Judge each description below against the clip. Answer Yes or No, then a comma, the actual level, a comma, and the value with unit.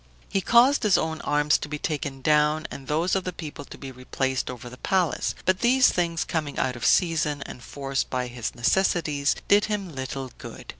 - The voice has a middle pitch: Yes, medium, 150 Hz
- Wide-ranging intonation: No, average, 5.0 semitones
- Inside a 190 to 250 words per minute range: Yes, average, 200 wpm